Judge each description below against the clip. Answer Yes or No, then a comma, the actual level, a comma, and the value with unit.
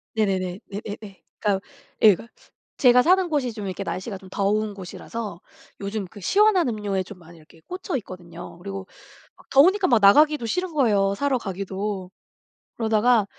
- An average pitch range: Yes, average, 4.5 semitones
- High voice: Yes, high, 210 Hz